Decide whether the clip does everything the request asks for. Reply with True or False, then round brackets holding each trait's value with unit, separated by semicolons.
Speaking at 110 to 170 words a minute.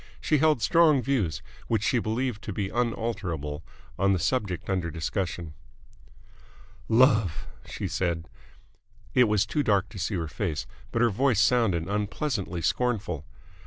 True (140 wpm)